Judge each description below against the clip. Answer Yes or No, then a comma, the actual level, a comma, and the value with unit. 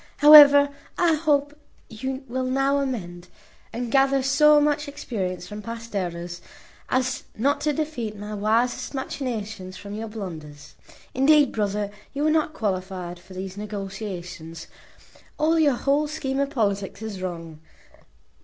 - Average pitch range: No, wide, 6.5 semitones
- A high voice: Yes, high, 230 Hz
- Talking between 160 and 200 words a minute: No, slow, 135 wpm